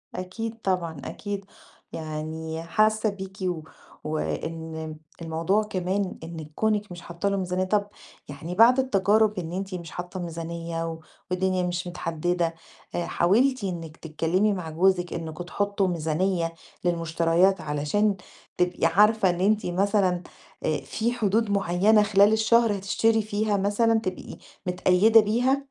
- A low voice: No, medium, 185 Hz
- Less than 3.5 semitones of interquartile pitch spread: No, average, 3.8 semitones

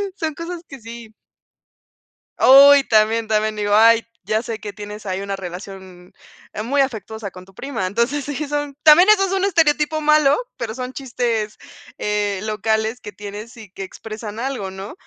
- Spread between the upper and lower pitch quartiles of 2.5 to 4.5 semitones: No, average, 5.0 semitones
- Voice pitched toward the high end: Yes, high, 225 Hz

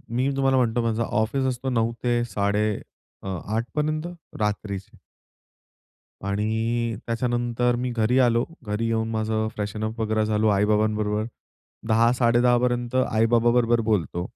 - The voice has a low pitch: Yes, low, 115 Hz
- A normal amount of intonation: No, narrow, 2.0 semitones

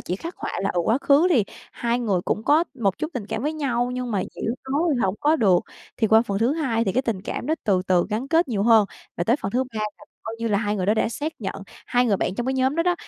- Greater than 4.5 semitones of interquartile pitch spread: Yes, average, 4.9 semitones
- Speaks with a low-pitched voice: No, high, 230 Hz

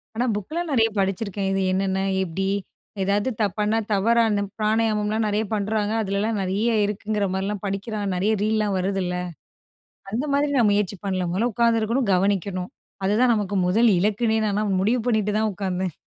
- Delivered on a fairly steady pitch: Yes, narrow, 2.2 semitones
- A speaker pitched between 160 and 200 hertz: No, high, 210 Hz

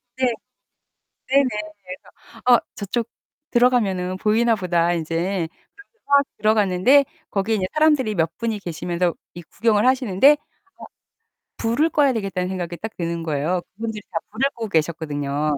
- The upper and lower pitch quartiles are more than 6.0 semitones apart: No, wide, 5.5 semitones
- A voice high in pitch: Yes, high, 205 Hz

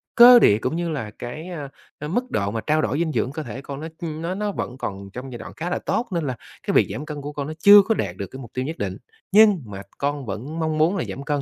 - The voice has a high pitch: No, medium, 150 Hz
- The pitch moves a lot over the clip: No, average, 5.0 semitones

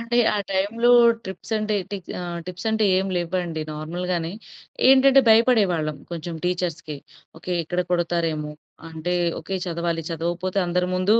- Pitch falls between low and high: Yes, medium, 180 Hz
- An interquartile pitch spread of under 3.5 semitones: Yes, average, 2.8 semitones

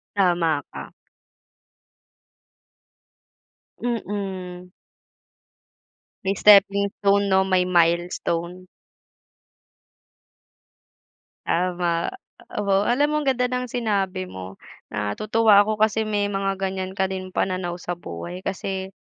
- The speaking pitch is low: No, high, 190 Hz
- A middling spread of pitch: No, narrow, 2.2 semitones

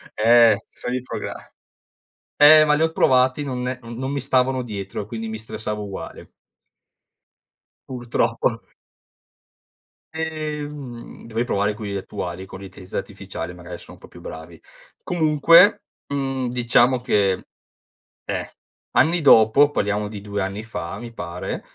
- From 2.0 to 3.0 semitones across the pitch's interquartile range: No, average, 5.0 semitones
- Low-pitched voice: Yes, low, 115 Hz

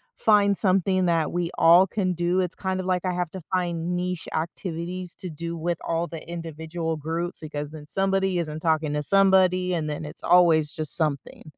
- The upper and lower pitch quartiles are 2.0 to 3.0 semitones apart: Yes, narrow, 2.5 semitones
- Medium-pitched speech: Yes, medium, 175 Hz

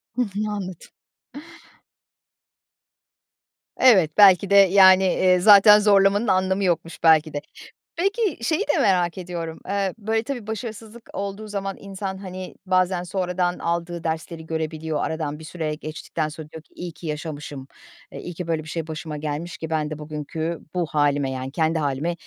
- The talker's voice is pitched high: No, medium, 175 Hz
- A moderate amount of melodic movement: Yes, average, 3.8 semitones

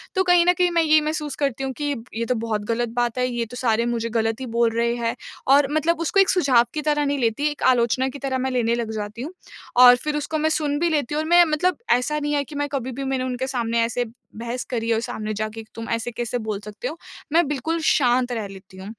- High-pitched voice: Yes, very high, 255 Hz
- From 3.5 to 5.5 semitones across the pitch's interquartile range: Yes, average, 4.4 semitones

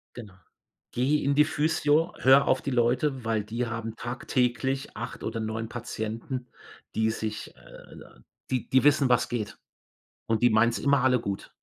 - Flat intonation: No, average, 3.1 semitones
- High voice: No, low, 120 Hz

